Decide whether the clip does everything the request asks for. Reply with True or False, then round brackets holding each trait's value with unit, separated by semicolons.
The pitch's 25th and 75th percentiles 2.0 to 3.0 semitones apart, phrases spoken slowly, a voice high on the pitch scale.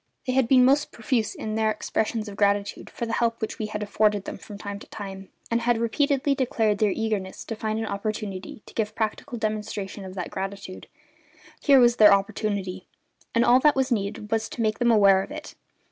False (2.6 semitones; 205 wpm; 215 Hz)